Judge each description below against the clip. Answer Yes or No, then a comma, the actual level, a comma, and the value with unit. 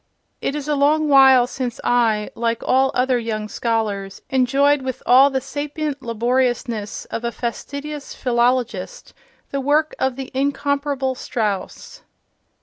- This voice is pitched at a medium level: No, very high, 260 Hz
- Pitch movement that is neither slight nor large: Yes, average, 3.1 semitones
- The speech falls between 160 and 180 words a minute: No, slow, 135 wpm